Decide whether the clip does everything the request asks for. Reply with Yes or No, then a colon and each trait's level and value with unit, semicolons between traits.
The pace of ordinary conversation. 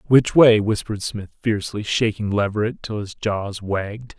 Yes: average, 160 wpm